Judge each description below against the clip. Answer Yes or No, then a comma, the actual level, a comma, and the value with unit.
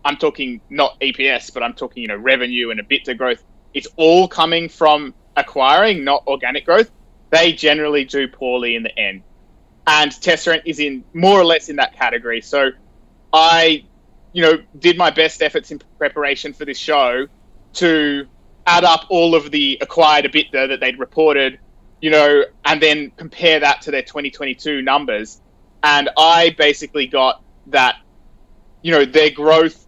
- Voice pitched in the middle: Yes, medium, 150 Hz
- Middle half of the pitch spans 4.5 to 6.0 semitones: No, average, 3.3 semitones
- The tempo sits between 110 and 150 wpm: No, average, 170 wpm